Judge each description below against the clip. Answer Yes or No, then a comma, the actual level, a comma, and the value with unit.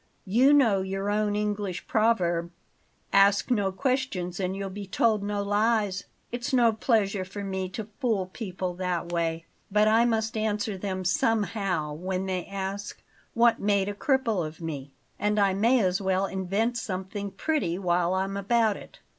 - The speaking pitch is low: No, high, 200 Hz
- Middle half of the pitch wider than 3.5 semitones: No, average, 2.9 semitones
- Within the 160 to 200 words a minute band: Yes, average, 165 wpm